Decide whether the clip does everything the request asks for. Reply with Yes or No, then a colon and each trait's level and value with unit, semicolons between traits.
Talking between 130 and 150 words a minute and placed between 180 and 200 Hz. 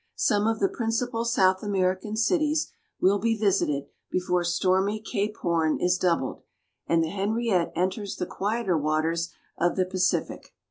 Yes: average, 145 wpm; high, 190 Hz